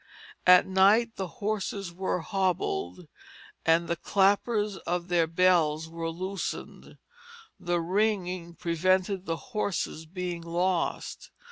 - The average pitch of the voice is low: No, medium, 180 Hz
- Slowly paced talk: Yes, slow, 110 wpm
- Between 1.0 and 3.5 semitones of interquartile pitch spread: Yes, narrow, 2.5 semitones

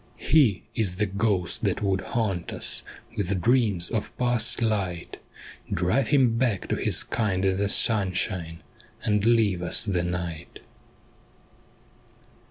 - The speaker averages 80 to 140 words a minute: Yes, slow, 135 wpm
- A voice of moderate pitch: No, low, 100 Hz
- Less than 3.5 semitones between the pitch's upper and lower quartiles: No, average, 4.0 semitones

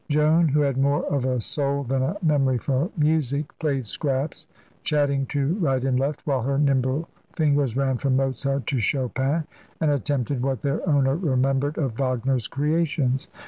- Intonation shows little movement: Yes, narrow, 2.0 semitones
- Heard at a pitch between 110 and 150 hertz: Yes, medium, 140 Hz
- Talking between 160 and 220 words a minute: Yes, average, 165 wpm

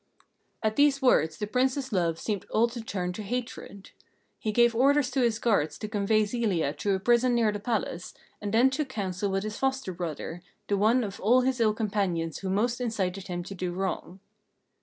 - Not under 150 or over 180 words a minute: No, average, 200 wpm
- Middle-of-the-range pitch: No, high, 210 Hz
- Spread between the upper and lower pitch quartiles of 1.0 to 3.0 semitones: No, average, 4.2 semitones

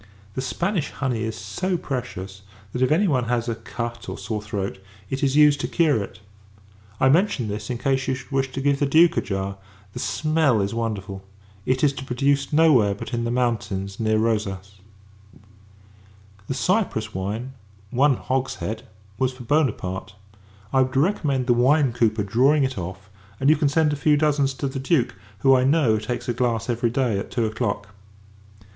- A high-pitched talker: No, low, 125 Hz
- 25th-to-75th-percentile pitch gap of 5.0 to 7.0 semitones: No, average, 4.4 semitones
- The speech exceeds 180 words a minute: Yes, average, 190 wpm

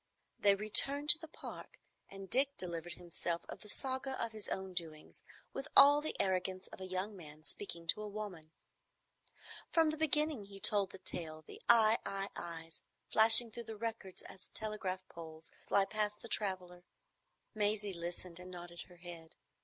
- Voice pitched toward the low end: No, high, 195 Hz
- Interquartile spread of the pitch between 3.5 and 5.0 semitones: Yes, average, 4.0 semitones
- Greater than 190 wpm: No, average, 165 wpm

